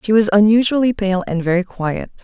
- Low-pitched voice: No, high, 205 Hz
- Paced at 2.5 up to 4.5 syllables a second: No, 5.5 syllables/s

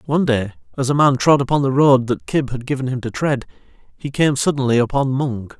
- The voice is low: Yes, low, 130 Hz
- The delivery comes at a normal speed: No, fast, 225 wpm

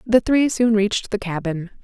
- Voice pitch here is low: No, high, 215 Hz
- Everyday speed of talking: Yes, average, 195 wpm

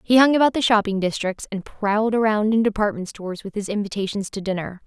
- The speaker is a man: No, female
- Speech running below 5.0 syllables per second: No, 6.1 syllables/s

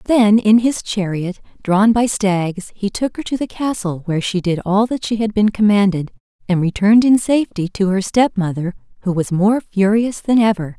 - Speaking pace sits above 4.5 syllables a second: Yes, 5.0 syllables/s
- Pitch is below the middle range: No, high, 205 Hz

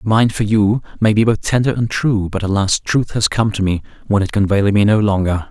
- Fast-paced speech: Yes, fast, 250 wpm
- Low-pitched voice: Yes, low, 105 Hz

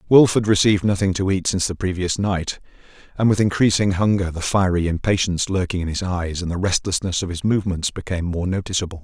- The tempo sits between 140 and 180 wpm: No, average, 200 wpm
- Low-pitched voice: Yes, very low, 95 Hz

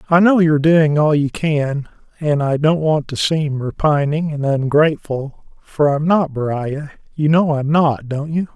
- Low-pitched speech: No, medium, 150 Hz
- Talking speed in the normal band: Yes, average, 170 wpm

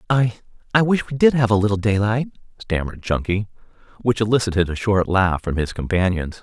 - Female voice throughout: No, male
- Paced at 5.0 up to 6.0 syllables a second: Yes, 5.6 syllables/s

